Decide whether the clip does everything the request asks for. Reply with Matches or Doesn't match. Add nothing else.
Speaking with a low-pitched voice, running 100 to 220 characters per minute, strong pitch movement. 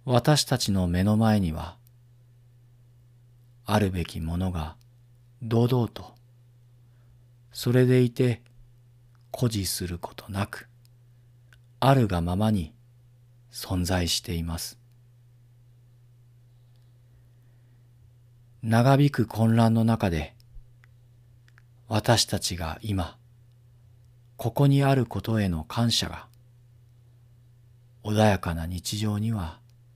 Doesn't match